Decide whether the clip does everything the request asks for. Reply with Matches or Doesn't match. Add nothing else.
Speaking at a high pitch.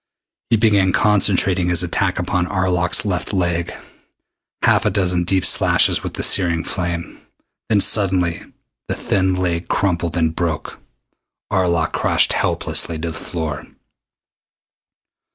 Doesn't match